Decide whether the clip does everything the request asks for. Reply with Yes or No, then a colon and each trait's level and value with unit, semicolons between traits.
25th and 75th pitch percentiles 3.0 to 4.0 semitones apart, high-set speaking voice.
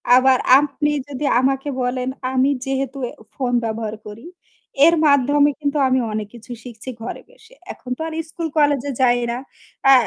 No: narrow, 2.6 semitones; very high, 265 Hz